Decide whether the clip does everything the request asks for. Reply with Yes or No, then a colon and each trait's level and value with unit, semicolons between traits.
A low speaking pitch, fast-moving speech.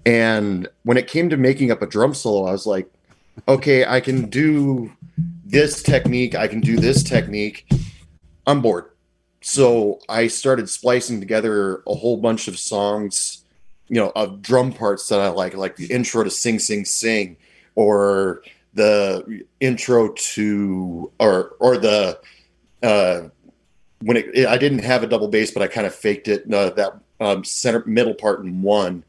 No: low, 110 Hz; average, 165 wpm